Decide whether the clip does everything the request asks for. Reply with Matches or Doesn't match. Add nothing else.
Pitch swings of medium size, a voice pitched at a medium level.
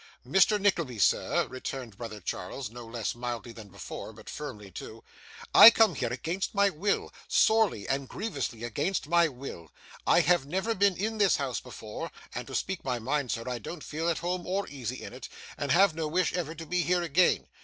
Doesn't match